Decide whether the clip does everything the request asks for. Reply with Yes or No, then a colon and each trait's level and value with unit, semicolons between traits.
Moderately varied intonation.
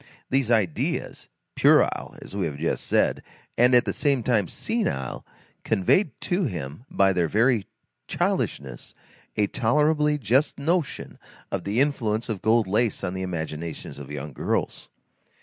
No: wide, 7.5 semitones